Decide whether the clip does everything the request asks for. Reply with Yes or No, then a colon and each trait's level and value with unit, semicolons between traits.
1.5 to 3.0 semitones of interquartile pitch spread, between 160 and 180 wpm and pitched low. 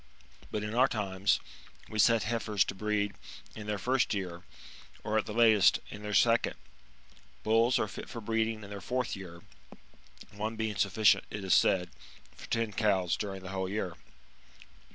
Yes: narrow, 2.5 semitones; average, 170 wpm; low, 105 Hz